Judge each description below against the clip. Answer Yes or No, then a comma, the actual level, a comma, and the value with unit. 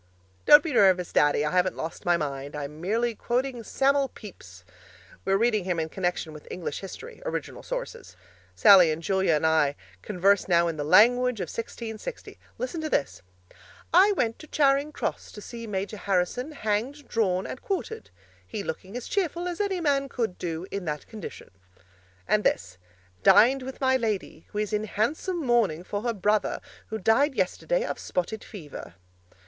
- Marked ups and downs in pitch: Yes, wide, 7.0 semitones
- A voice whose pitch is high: Yes, high, 215 Hz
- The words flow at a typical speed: Yes, average, 170 wpm